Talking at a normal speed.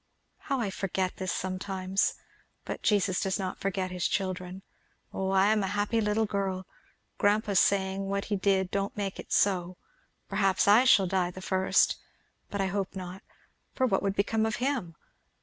Yes: average, 170 wpm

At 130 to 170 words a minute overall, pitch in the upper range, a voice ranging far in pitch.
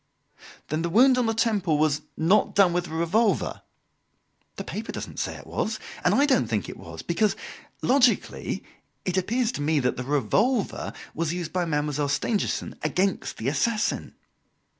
No: average, 165 wpm; medium, 175 Hz; wide, 6.8 semitones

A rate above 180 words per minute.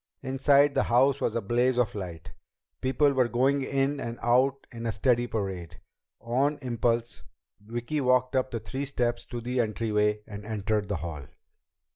No: average, 170 wpm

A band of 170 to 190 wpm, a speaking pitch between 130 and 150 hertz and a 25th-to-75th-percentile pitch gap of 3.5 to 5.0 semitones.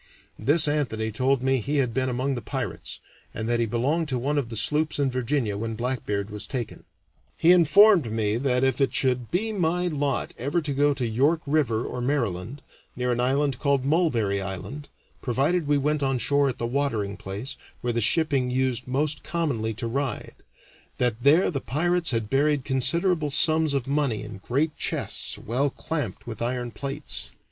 Yes: average, 185 wpm; low, 135 Hz; average, 3.8 semitones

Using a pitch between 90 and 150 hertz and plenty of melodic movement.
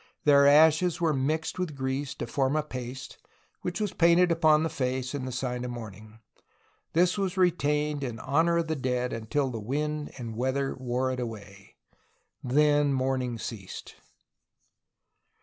No: low, 135 Hz; average, 3.7 semitones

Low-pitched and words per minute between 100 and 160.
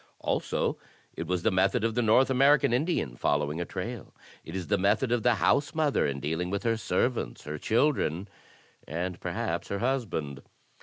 No: low, 100 Hz; average, 175 wpm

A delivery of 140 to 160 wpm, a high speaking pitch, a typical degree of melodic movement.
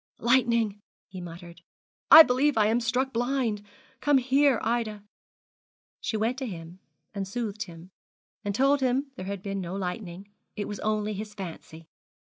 Yes: average, 155 wpm; high, 215 Hz; average, 4.3 semitones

